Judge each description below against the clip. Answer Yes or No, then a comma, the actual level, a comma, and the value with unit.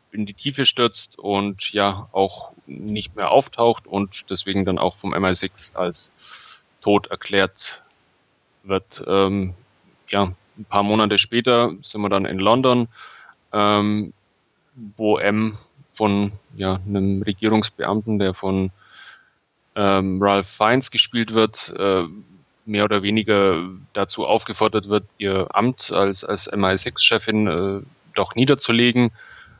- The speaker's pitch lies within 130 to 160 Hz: No, low, 105 Hz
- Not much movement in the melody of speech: Yes, narrow, 2.1 semitones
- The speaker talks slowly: Yes, slow, 120 wpm